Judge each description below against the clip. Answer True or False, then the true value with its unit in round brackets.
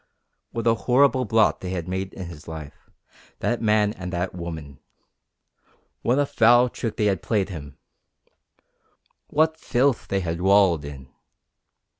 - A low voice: True (95 Hz)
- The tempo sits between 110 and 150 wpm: True (145 wpm)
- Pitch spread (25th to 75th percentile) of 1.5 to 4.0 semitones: False (5.5 semitones)